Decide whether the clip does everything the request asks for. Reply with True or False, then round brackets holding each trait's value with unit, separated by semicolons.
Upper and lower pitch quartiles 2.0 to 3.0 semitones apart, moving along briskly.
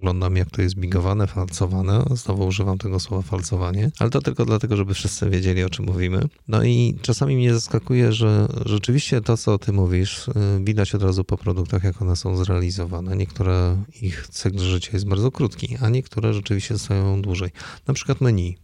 False (3.7 semitones; 180 wpm)